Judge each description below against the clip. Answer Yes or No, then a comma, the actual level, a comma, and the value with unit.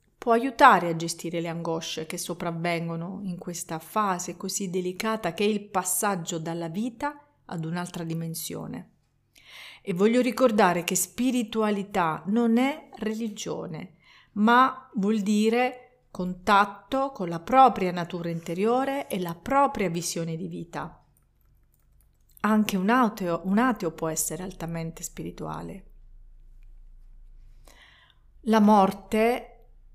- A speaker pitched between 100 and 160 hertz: No, medium, 185 Hz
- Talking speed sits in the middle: No, slow, 110 wpm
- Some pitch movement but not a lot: Yes, average, 5.0 semitones